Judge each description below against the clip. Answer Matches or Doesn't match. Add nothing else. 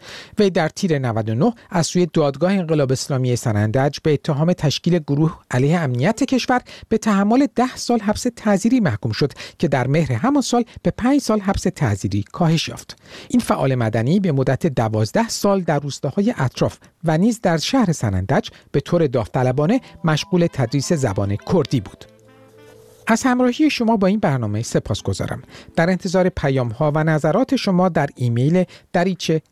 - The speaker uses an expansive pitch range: Matches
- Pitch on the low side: Doesn't match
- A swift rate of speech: Matches